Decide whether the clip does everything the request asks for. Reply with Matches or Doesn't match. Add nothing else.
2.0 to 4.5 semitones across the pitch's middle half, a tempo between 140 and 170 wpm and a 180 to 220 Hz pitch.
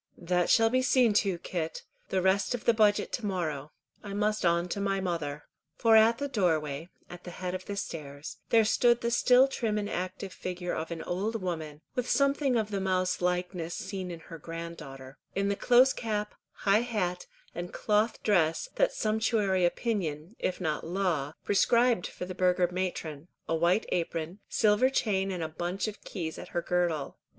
Doesn't match